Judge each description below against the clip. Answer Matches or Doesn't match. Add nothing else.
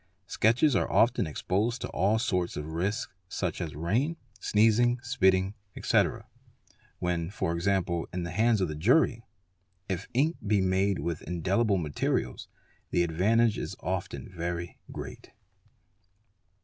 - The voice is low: Matches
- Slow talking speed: Matches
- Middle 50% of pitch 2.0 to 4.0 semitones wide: Doesn't match